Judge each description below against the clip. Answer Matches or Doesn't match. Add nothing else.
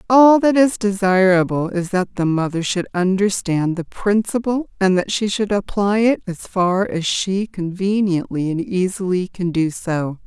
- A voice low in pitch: Doesn't match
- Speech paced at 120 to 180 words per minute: Matches